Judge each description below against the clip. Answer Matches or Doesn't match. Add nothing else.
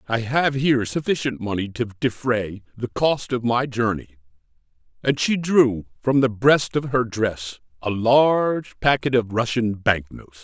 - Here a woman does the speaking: Doesn't match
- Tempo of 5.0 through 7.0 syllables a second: Doesn't match